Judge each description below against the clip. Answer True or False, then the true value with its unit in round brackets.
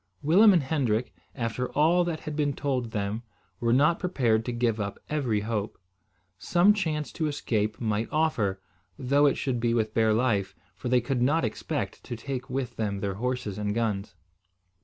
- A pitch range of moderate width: True (5.0 semitones)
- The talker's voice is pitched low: True (125 Hz)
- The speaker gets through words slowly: False (180 wpm)